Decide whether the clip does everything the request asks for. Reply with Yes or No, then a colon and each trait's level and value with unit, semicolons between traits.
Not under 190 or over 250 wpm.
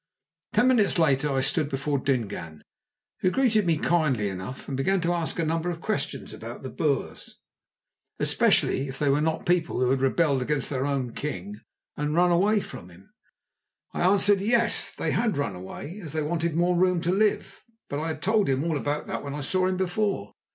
Yes: average, 200 wpm